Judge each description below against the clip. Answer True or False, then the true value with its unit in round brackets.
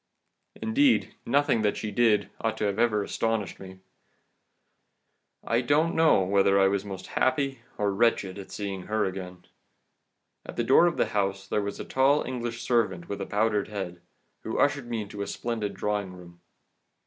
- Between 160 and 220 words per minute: True (170 wpm)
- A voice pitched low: True (105 Hz)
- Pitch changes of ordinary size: True (3.5 semitones)